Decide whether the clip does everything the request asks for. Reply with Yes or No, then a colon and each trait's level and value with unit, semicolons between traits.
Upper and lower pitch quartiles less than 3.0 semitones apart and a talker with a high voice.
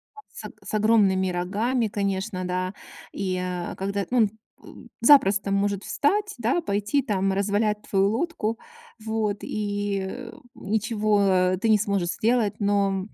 Yes: narrow, 2.4 semitones; high, 205 Hz